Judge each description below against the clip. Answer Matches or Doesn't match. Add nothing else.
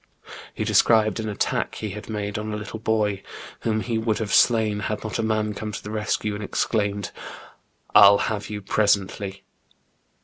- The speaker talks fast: Doesn't match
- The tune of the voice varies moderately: Doesn't match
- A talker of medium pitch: Doesn't match